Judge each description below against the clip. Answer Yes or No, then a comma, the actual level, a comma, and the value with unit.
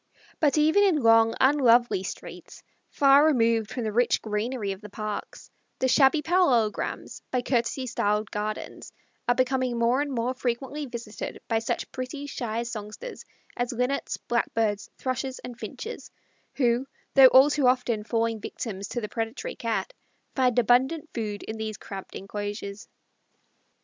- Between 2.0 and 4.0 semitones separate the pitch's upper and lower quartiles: Yes, average, 3.2 semitones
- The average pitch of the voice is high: Yes, high, 240 Hz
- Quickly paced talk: No, average, 145 wpm